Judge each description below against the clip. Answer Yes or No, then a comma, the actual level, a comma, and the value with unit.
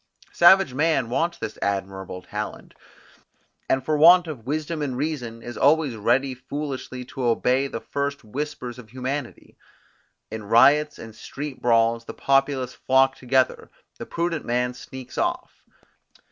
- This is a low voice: Yes, low, 130 Hz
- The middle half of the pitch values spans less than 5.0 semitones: Yes, average, 3.7 semitones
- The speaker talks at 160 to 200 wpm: No, average, 140 wpm